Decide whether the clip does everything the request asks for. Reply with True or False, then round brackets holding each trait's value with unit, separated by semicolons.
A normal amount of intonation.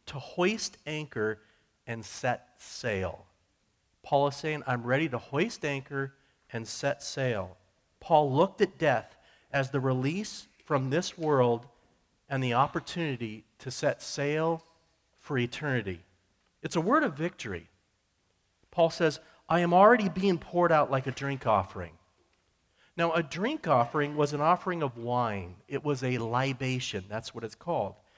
False (6.4 semitones)